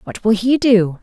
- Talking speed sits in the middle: No, fast, 235 wpm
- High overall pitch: Yes, high, 220 Hz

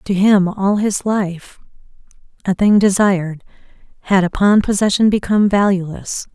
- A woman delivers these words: Yes, female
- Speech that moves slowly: Yes, slow, 125 wpm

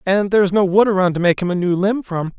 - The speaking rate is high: Yes, fast, 325 wpm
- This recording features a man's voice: Yes, male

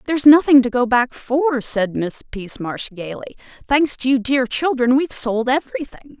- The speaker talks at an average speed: Yes, average, 175 wpm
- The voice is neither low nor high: No, very high, 255 Hz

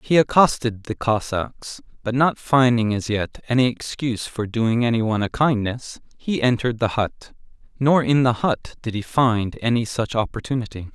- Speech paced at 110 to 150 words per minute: No, average, 165 wpm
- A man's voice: Yes, male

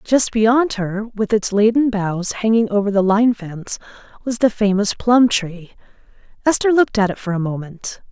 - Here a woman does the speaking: Yes, female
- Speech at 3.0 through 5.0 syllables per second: Yes, 4.7 syllables/s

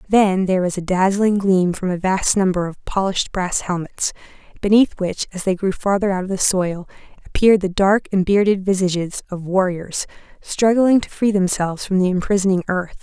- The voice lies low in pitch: No, high, 190 Hz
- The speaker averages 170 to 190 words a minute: Yes, average, 185 wpm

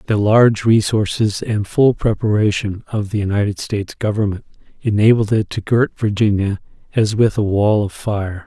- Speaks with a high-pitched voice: No, low, 105 Hz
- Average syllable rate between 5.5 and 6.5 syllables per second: No, 5.0 syllables/s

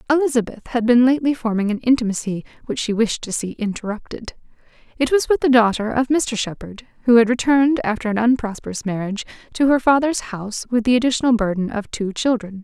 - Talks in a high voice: Yes, high, 235 Hz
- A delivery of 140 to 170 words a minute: No, average, 185 wpm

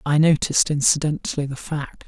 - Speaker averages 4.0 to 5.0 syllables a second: No, 5.6 syllables/s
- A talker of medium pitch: Yes, medium, 145 Hz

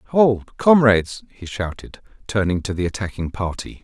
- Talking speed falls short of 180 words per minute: Yes, average, 140 wpm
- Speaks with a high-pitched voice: No, low, 105 Hz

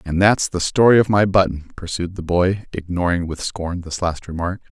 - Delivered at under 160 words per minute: No, average, 200 wpm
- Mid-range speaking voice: No, very low, 90 Hz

